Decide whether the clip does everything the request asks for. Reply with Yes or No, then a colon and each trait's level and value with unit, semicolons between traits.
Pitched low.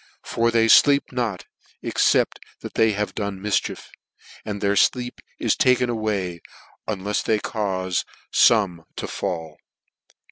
Yes: low, 105 Hz